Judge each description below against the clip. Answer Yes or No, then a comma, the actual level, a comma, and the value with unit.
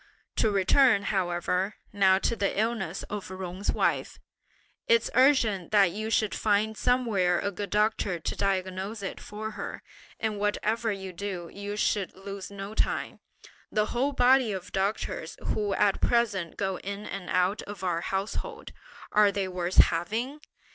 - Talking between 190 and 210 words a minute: No, average, 155 wpm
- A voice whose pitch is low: No, high, 200 Hz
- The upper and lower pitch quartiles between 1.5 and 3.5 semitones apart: Yes, narrow, 2.5 semitones